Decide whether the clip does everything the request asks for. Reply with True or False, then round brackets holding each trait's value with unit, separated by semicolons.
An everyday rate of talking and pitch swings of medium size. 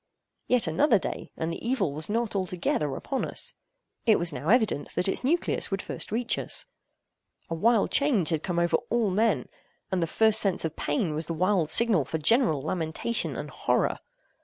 False (185 wpm; 6.1 semitones)